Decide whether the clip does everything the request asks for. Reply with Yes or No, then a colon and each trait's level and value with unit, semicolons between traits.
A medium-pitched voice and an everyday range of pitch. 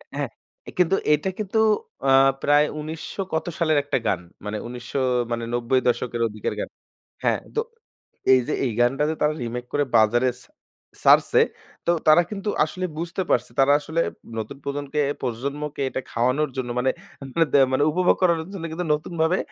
Yes: medium, 145 Hz; average, 4.7 semitones